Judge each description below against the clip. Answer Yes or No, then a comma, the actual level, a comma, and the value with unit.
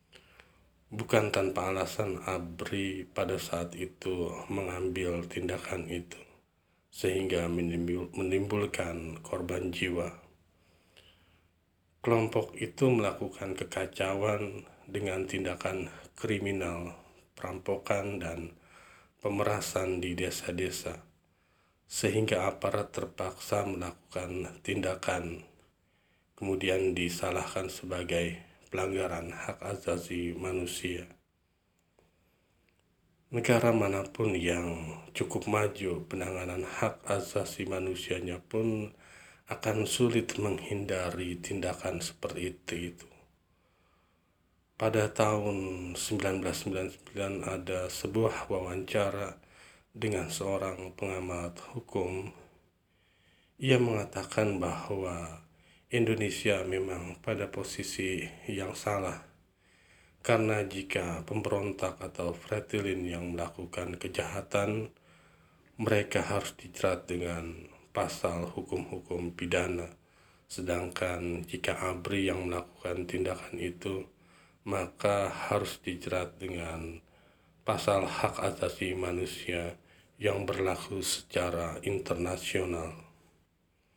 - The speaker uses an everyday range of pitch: No, narrow, 2.1 semitones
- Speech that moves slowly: Yes, slow, 75 wpm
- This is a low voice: Yes, very low, 90 Hz